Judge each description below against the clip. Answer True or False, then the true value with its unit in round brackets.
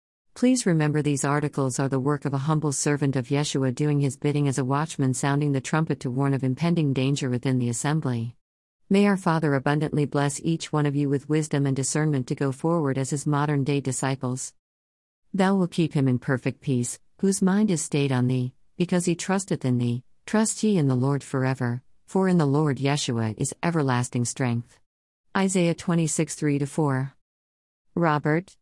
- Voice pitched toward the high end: False (140 Hz)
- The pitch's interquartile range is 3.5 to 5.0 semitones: False (3.1 semitones)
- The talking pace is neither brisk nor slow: True (185 wpm)